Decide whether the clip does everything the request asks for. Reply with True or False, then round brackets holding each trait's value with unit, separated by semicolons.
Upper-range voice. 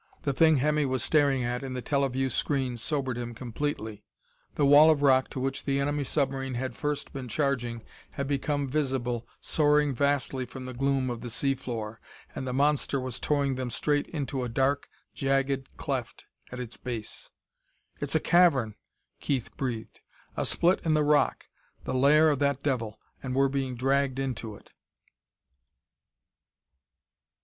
False (135 Hz)